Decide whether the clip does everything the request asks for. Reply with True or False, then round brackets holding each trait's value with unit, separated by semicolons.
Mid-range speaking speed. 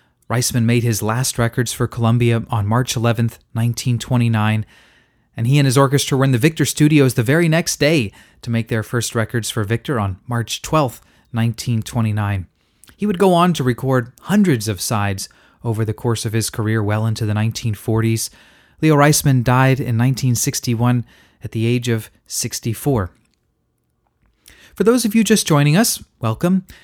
True (165 wpm)